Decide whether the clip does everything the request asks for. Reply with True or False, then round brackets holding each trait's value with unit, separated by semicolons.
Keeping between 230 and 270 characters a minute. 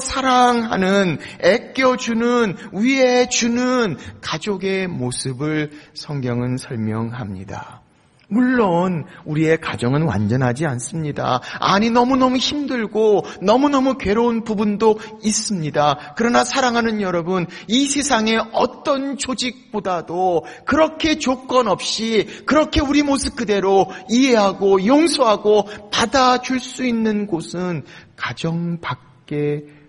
True (245 characters per minute)